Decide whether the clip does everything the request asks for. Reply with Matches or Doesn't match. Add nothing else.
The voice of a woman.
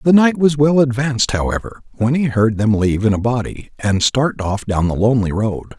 Doesn't match